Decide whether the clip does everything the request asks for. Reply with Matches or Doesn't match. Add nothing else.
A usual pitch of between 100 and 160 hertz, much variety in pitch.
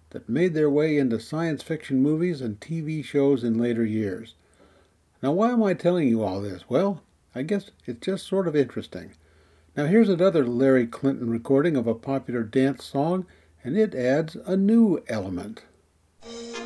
Matches